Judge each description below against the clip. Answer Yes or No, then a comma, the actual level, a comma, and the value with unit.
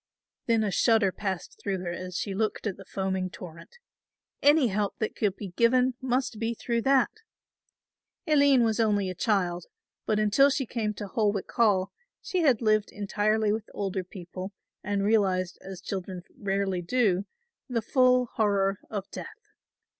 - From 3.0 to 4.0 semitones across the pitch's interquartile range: Yes, average, 3.5 semitones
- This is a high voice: Yes, high, 210 Hz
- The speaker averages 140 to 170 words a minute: Yes, average, 160 wpm